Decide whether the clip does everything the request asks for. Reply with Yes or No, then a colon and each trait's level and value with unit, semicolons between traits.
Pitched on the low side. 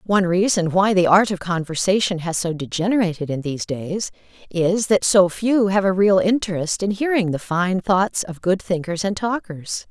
No: medium, 185 Hz